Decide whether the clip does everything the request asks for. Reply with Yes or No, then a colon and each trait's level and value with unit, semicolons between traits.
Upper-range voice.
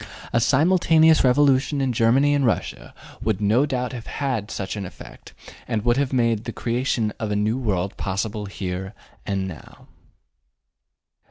No: low, 115 Hz